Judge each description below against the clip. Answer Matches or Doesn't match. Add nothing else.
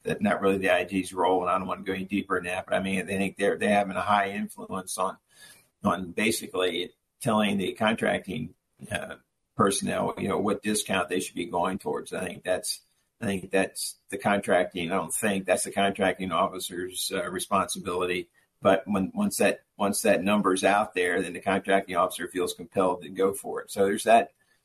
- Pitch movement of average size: Doesn't match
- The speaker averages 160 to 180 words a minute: Doesn't match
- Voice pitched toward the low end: Matches